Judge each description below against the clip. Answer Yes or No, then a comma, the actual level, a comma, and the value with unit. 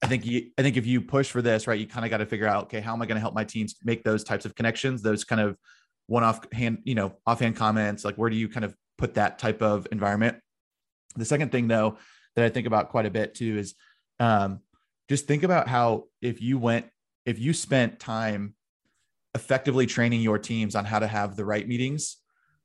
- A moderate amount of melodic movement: No, narrow, 2.3 semitones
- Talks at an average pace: No, fast, 235 wpm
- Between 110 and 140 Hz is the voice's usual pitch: Yes, low, 115 Hz